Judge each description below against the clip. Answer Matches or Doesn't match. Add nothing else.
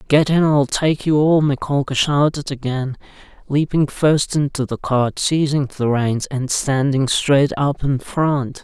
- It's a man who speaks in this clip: Matches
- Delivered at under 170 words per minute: Matches